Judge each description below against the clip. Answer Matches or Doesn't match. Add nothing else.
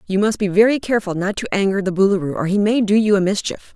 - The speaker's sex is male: Doesn't match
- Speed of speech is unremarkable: Doesn't match